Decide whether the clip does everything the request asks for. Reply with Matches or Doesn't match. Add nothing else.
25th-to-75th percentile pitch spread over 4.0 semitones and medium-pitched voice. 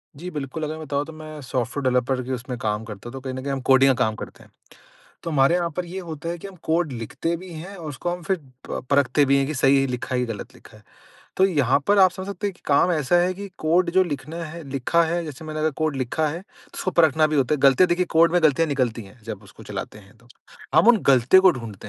Matches